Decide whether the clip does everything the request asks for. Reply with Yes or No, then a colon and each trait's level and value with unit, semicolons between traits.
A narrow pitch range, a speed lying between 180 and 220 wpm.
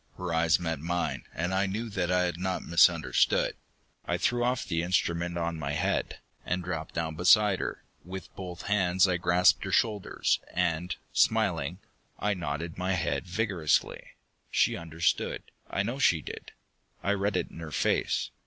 No: narrow, 2.3 semitones; average, 165 wpm